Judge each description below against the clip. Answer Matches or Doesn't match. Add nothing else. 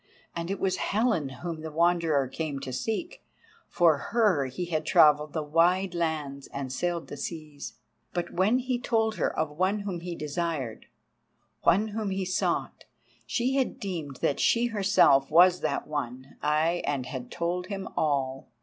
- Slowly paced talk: Doesn't match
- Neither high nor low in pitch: Matches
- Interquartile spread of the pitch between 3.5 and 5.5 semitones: Matches